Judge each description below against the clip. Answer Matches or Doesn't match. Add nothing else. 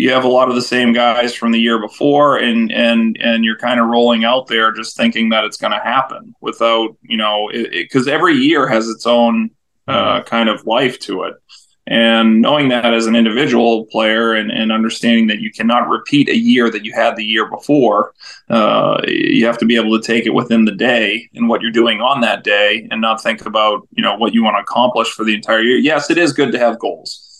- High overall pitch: Doesn't match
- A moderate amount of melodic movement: Doesn't match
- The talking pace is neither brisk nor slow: Doesn't match